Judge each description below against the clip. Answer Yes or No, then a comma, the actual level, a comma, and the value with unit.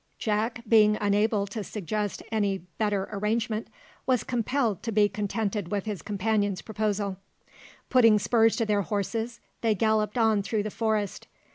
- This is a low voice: No, high, 215 Hz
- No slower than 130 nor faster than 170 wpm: Yes, average, 145 wpm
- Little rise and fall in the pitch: Yes, narrow, 1.7 semitones